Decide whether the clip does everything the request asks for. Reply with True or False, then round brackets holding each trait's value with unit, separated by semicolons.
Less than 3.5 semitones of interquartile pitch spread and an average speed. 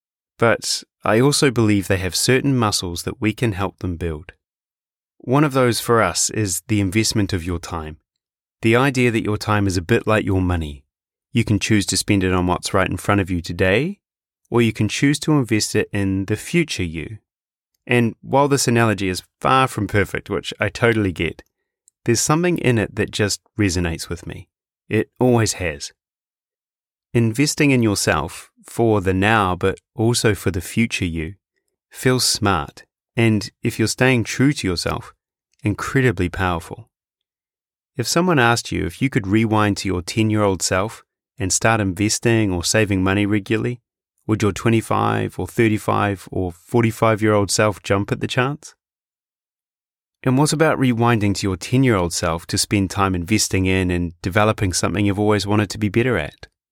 False (3.8 semitones; 180 wpm)